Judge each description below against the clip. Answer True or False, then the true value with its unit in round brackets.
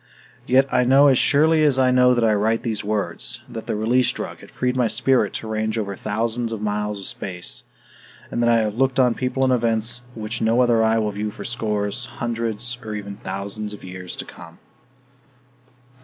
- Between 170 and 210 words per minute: True (200 wpm)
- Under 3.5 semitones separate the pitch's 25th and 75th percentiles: True (2.8 semitones)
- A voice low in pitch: True (115 Hz)